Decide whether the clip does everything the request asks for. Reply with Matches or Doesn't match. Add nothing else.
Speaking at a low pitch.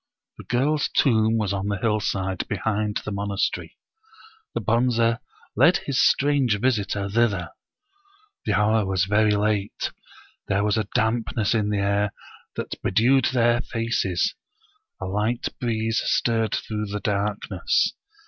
Matches